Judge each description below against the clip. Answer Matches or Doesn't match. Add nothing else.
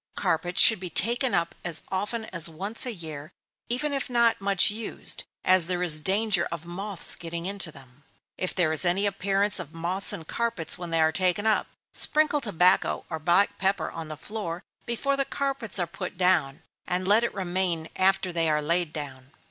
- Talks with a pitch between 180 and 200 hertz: Matches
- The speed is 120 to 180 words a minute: Doesn't match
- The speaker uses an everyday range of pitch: Matches